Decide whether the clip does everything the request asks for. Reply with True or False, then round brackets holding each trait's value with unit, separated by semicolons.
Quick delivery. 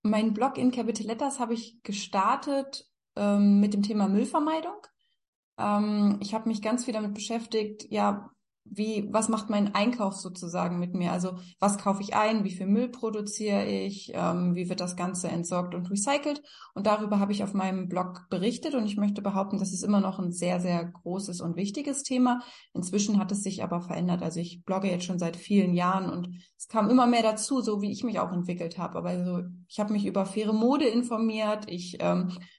True (200 wpm)